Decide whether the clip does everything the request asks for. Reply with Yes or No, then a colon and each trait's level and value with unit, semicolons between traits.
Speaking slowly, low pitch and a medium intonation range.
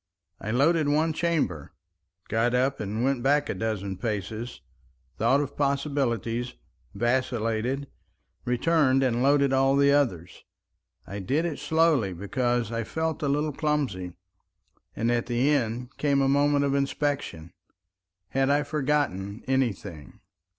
Yes: slow, 130 wpm; low, 130 Hz; average, 4.4 semitones